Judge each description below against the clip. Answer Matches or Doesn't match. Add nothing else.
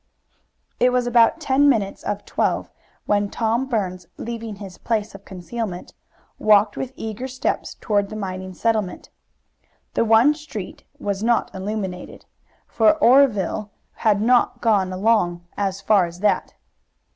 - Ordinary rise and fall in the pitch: Matches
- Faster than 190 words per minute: Doesn't match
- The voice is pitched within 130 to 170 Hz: Doesn't match